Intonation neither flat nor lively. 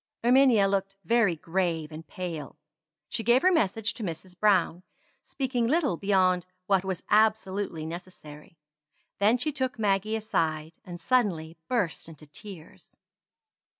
Yes: average, 5.0 semitones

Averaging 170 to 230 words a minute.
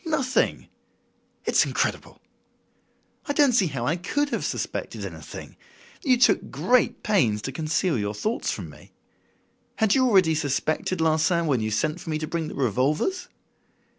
No: average, 155 wpm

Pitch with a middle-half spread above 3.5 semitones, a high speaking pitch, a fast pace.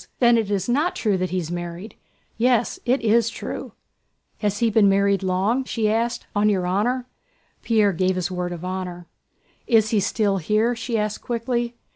No: average, 3.9 semitones; high, 210 Hz; average, 175 wpm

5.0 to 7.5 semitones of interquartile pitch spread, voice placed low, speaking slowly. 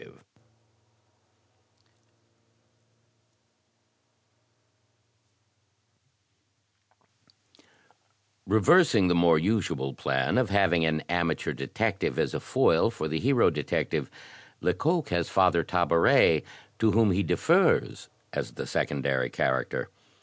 Yes: average, 5.3 semitones; very low, 85 Hz; slow, 85 wpm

